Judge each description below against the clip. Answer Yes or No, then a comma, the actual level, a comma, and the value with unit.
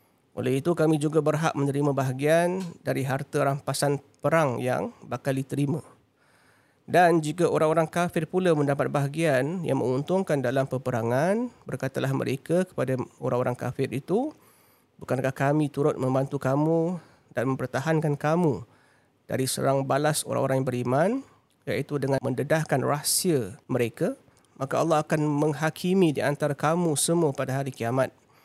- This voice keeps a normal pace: Yes, average, 130 wpm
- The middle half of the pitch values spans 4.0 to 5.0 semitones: No, average, 3.3 semitones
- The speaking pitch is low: No, medium, 145 Hz